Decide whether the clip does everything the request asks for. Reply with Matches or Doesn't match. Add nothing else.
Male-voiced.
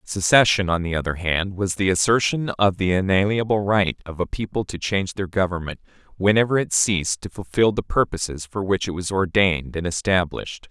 Matches